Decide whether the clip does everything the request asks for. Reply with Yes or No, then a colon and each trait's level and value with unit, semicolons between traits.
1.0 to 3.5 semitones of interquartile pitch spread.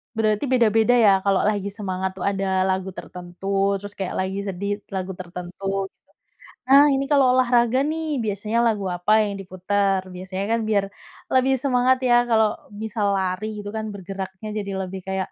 Yes: average, 2.9 semitones